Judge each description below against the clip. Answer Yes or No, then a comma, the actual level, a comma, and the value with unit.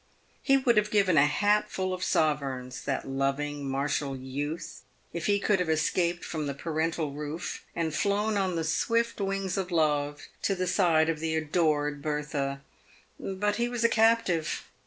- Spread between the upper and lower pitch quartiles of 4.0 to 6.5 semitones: Yes, average, 5.0 semitones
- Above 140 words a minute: Yes, average, 170 wpm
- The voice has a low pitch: No, medium, 165 Hz